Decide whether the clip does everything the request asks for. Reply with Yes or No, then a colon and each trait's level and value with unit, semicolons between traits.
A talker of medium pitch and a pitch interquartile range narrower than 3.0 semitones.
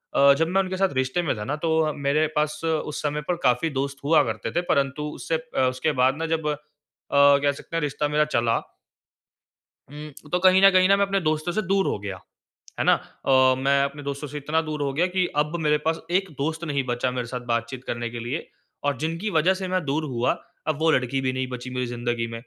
No: medium, 150 Hz; average, 3.8 semitones